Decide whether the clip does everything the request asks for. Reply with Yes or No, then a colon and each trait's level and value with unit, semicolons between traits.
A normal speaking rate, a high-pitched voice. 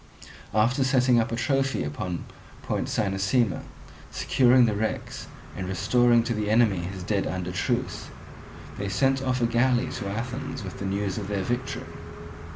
No: average, 160 wpm; low, 110 Hz